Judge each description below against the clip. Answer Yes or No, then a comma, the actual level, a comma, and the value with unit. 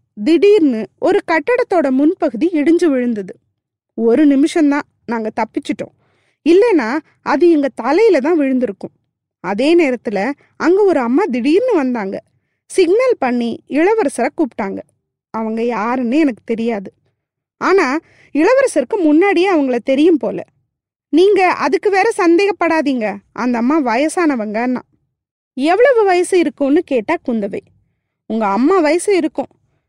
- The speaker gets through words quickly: No, average, 110 wpm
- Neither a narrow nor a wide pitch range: No, wide, 6.6 semitones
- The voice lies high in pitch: Yes, very high, 295 Hz